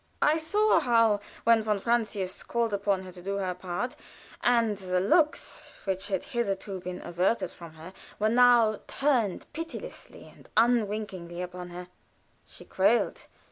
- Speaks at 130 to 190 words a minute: Yes, average, 145 wpm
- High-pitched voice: Yes, high, 205 Hz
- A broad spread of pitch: No, average, 4.3 semitones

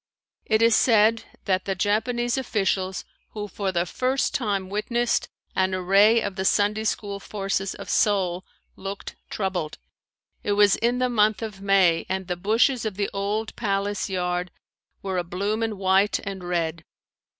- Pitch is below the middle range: No, high, 200 Hz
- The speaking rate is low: No, average, 155 wpm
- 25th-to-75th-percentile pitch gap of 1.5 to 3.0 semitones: Yes, narrow, 2.5 semitones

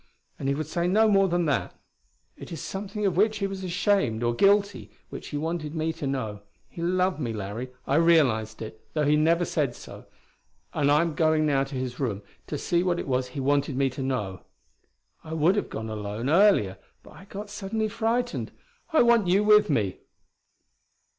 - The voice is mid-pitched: Yes, medium, 155 Hz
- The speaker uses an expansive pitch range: Yes, wide, 7.0 semitones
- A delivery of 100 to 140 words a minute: No, average, 195 wpm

